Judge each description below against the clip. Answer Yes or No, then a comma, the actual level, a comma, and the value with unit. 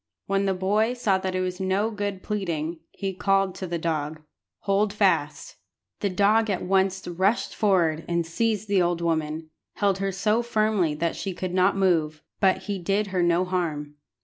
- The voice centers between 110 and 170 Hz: No, high, 190 Hz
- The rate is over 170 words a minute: Yes, average, 180 wpm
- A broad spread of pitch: No, average, 2.8 semitones